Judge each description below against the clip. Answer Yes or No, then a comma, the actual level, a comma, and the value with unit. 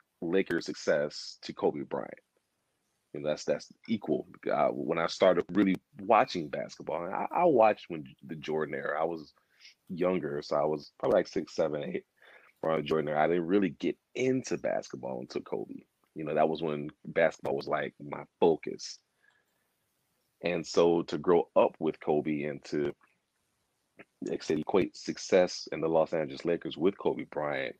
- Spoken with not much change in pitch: Yes, narrow, 2.2 semitones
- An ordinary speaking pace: Yes, average, 165 wpm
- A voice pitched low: Yes, very low, 80 Hz